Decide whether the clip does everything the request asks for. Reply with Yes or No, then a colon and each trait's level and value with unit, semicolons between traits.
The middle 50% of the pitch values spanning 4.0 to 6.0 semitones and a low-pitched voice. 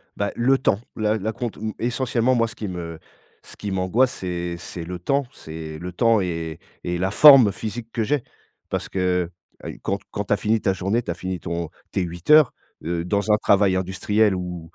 Yes: average, 4.4 semitones; very low, 95 Hz